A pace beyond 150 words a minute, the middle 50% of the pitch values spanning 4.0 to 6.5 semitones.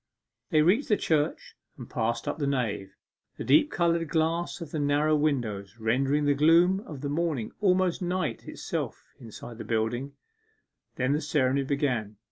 Yes: average, 160 wpm; average, 5.1 semitones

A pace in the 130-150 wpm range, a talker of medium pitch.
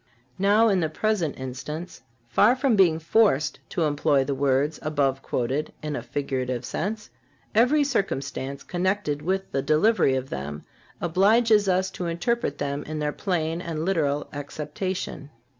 Yes: average, 145 wpm; medium, 155 Hz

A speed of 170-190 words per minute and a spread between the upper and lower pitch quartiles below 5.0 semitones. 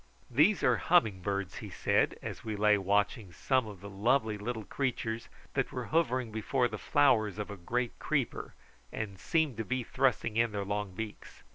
Yes: average, 180 wpm; average, 3.9 semitones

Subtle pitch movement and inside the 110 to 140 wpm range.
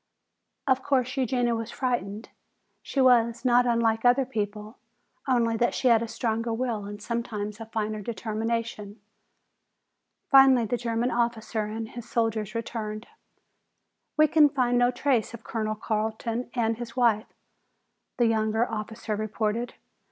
Yes: narrow, 2.0 semitones; slow, 135 wpm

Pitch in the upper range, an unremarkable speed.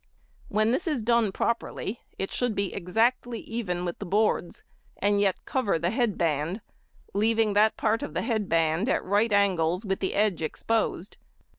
Yes: high, 205 Hz; average, 170 wpm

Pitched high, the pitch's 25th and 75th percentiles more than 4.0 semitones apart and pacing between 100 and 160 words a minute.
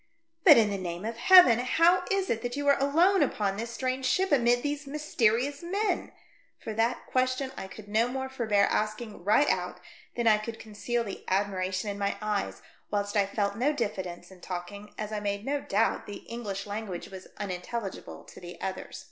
No: high, 225 Hz; average, 4.6 semitones; average, 200 wpm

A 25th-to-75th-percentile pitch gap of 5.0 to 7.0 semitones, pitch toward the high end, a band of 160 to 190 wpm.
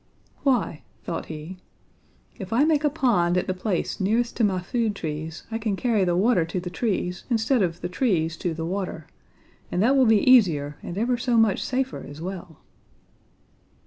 Yes: average, 5.3 semitones; high, 195 Hz; average, 185 wpm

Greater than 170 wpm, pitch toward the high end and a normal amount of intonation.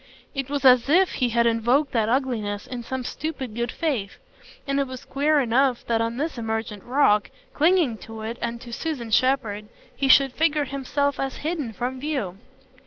Yes: average, 180 wpm; very high, 255 Hz; average, 3.6 semitones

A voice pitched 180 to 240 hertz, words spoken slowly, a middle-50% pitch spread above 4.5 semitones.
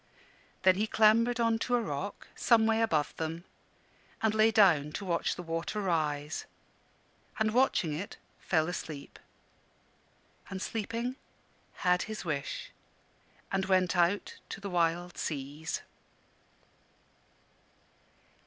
Yes: medium, 185 Hz; slow, 115 wpm; average, 5.1 semitones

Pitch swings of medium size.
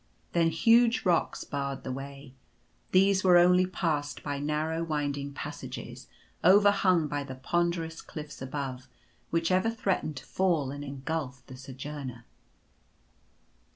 Yes: average, 4.3 semitones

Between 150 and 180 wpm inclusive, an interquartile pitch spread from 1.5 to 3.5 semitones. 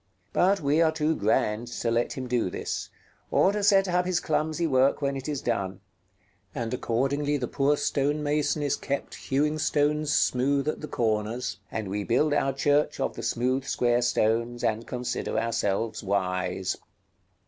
No: average, 170 wpm; average, 4.4 semitones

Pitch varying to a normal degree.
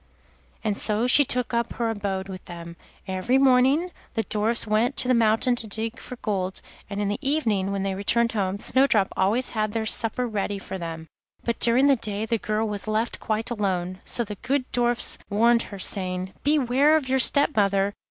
Yes: average, 3.7 semitones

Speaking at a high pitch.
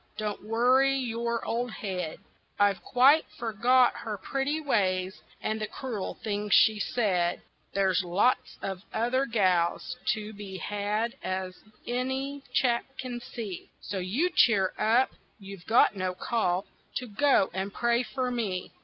Yes: high, 220 Hz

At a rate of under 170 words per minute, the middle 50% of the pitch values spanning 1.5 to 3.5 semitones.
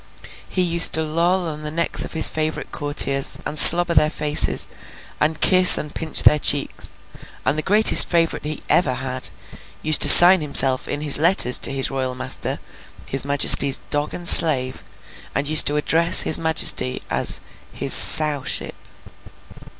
Yes: average, 160 wpm; average, 3.0 semitones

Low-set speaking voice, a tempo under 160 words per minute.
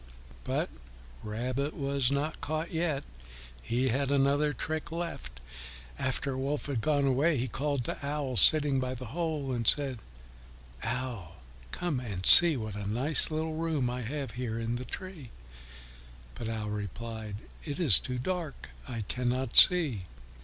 Yes: low, 130 Hz; average, 150 wpm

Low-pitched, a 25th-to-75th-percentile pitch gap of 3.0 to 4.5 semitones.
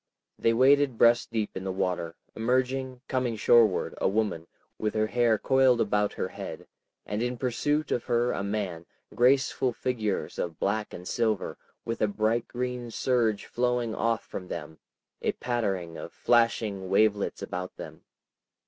Yes: low, 115 Hz; average, 3.3 semitones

